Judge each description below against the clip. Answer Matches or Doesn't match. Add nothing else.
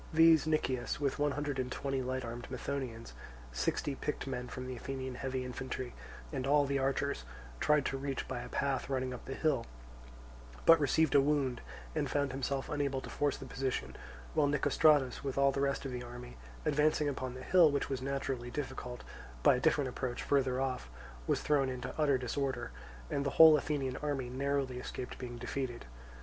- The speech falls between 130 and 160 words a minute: Doesn't match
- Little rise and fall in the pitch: Matches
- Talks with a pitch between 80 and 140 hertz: Matches